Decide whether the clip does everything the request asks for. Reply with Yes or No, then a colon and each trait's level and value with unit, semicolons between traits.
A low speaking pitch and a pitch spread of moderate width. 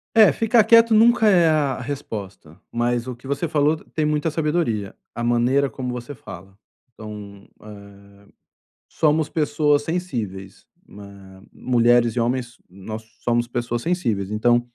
No: low, 120 Hz; wide, 6.0 semitones